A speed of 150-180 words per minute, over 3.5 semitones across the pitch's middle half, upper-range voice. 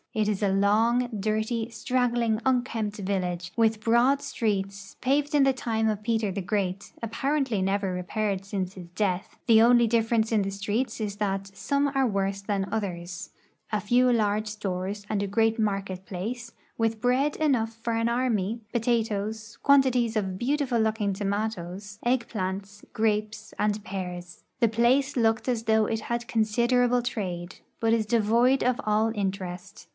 No: average, 160 wpm; average, 3.1 semitones; high, 220 Hz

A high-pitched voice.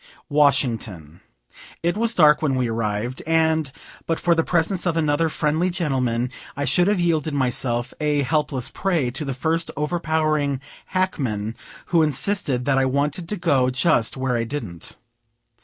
No: medium, 145 Hz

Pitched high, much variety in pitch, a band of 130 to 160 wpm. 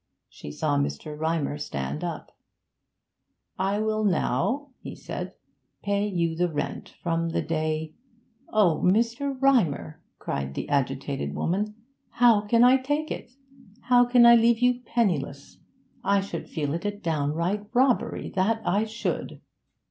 Yes: high, 200 Hz; wide, 6.9 semitones; average, 140 wpm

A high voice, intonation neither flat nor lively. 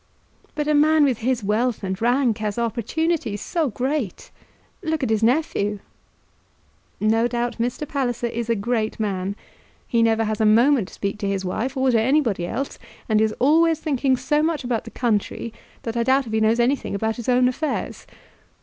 Yes: high, 235 Hz; average, 3.8 semitones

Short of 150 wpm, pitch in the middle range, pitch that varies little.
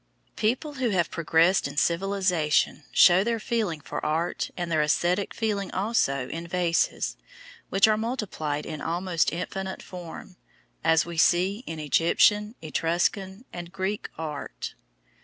No: slow, 135 wpm; medium, 175 Hz; average, 3.6 semitones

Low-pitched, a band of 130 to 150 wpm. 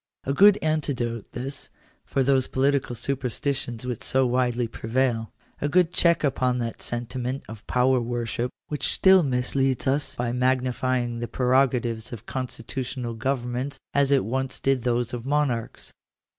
Yes: low, 125 Hz; average, 145 wpm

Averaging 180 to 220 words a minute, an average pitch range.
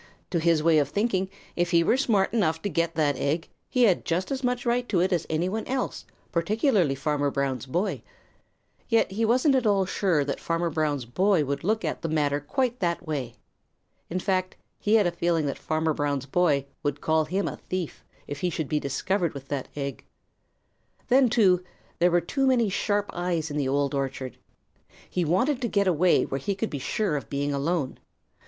No: average, 200 wpm; wide, 5.7 semitones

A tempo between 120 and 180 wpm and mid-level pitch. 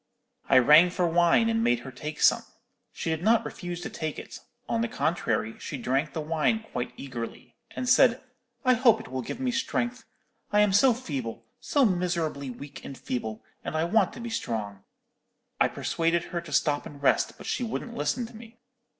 No: average, 195 wpm; medium, 170 Hz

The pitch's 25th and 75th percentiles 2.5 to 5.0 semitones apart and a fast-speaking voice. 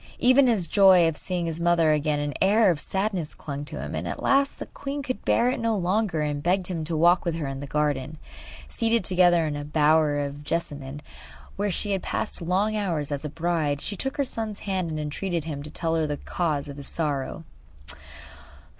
Yes: average, 4.6 semitones; fast, 215 wpm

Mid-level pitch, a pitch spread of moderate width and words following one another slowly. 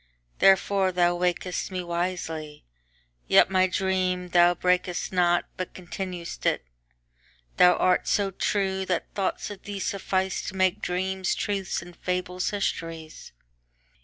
No: medium, 180 Hz; narrow, 1.5 semitones; slow, 115 wpm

